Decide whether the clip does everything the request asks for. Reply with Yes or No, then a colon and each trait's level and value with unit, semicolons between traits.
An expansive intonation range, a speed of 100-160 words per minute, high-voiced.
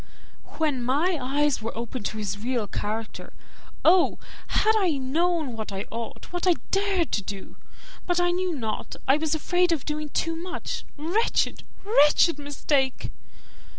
Yes: wide, 6.6 semitones; average, 150 wpm; very high, 295 Hz